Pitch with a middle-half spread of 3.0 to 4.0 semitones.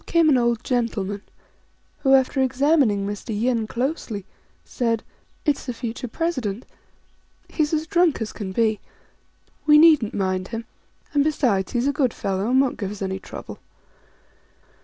No: average, 5.3 semitones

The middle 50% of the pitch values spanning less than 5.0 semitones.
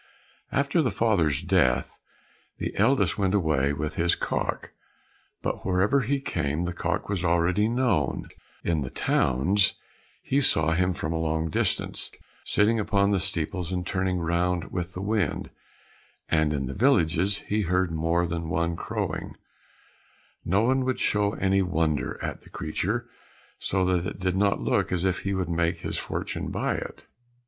Yes: average, 3.6 semitones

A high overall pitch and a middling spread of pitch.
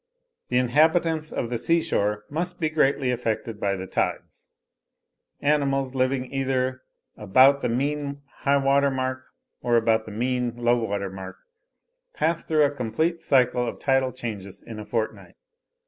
No: low, 130 Hz; average, 3.5 semitones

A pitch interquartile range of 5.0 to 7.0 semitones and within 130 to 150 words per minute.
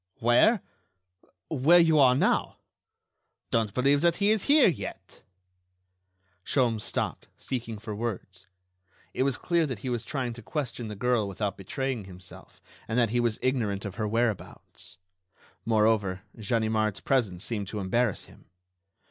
No: average, 4.0 semitones; average, 145 wpm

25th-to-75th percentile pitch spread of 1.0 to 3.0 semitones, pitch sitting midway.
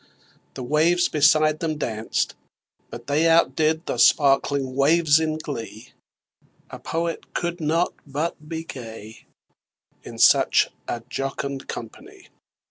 No: average, 3.8 semitones; medium, 150 Hz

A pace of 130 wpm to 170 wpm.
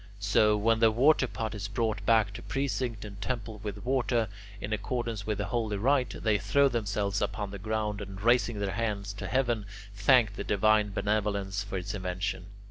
No: average, 180 wpm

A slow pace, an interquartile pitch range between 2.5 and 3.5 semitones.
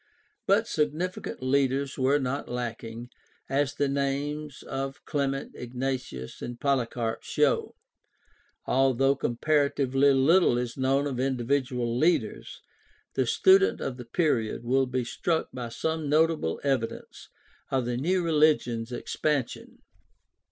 Yes: slow, 115 wpm; average, 3.0 semitones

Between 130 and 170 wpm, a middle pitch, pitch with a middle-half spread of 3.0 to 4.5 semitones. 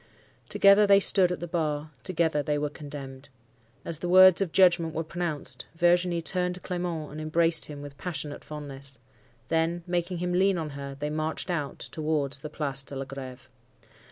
No: average, 180 wpm; medium, 160 Hz; average, 3.4 semitones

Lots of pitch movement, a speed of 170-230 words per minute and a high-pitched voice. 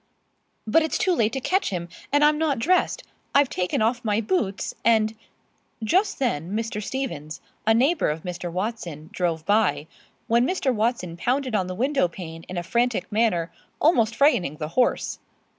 Yes: wide, 6.8 semitones; average, 175 wpm; high, 220 Hz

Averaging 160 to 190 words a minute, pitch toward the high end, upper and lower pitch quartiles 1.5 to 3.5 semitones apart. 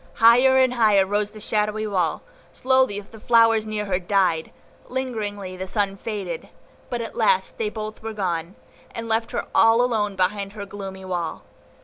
Yes: average, 165 wpm; high, 210 Hz; average, 2.8 semitones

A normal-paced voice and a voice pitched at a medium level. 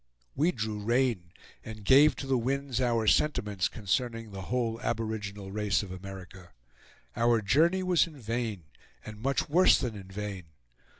No: average, 155 wpm; low, 115 Hz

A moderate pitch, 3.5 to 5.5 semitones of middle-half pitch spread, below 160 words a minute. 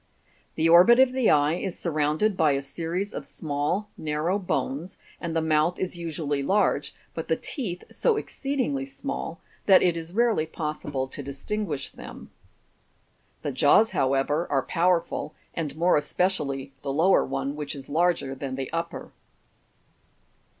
Yes: medium, 165 Hz; average, 4.4 semitones; average, 150 wpm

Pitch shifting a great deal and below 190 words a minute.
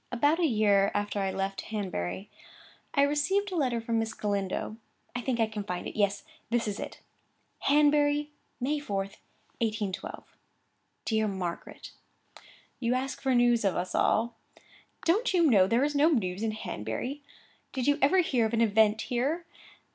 Yes: wide, 5.8 semitones; average, 160 wpm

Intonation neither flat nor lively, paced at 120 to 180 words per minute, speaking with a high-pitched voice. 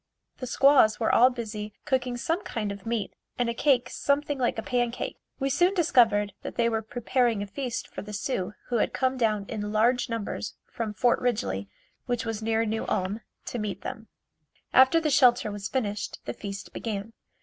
No: average, 3.3 semitones; average, 190 wpm; high, 230 Hz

